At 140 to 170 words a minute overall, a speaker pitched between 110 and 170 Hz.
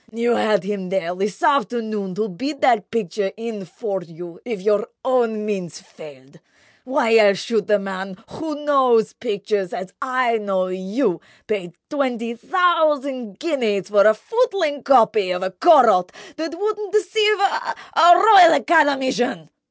No: average, 145 wpm; high, 225 Hz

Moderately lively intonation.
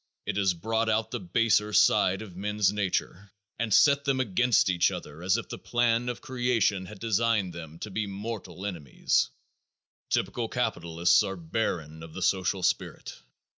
Yes: average, 4.1 semitones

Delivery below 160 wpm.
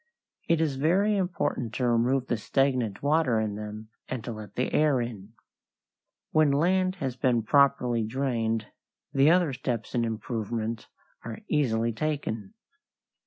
Yes: average, 140 wpm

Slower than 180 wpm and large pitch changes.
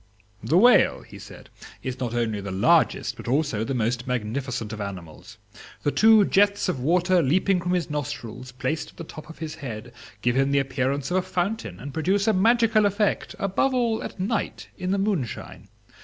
No: average, 190 wpm; wide, 7.7 semitones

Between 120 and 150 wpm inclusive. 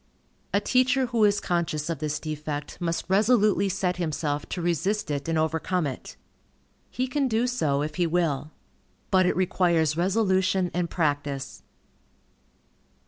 Yes: average, 140 wpm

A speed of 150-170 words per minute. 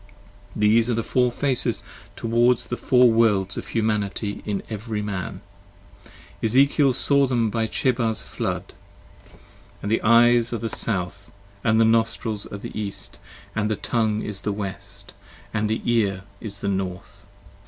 Yes: average, 155 wpm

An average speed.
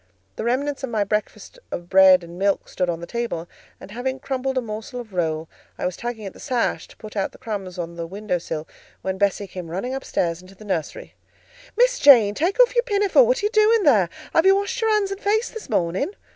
No: fast, 230 wpm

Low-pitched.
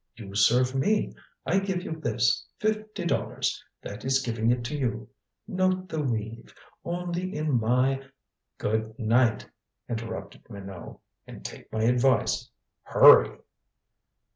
Yes: low, 125 Hz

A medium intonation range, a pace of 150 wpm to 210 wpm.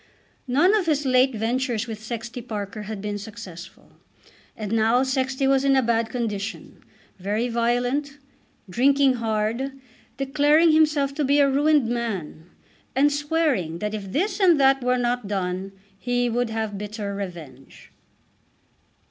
No: average, 4.5 semitones; average, 140 wpm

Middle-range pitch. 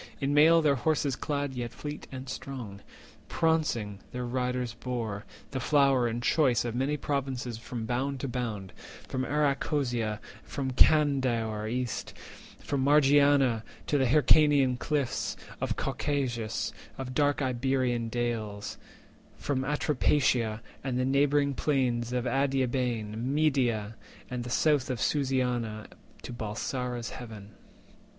No: low, 130 Hz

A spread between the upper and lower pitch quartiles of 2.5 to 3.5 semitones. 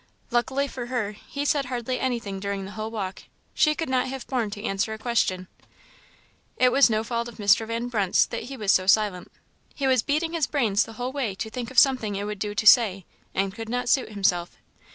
No: average, 4.0 semitones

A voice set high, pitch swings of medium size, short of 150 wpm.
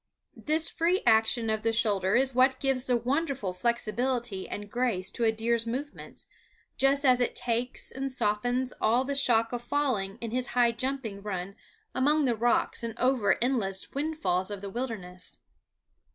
No: high, 240 Hz; average, 3.4 semitones; average, 165 wpm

